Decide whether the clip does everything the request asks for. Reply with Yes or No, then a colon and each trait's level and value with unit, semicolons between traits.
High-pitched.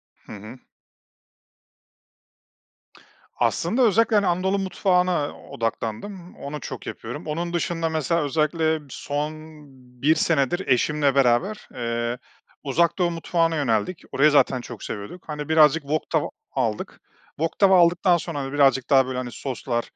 No: medium, 155 Hz